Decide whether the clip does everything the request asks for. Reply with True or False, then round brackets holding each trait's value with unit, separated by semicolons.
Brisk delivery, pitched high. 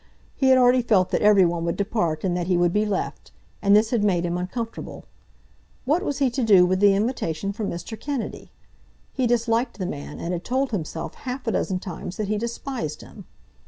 True (210 wpm; 205 Hz)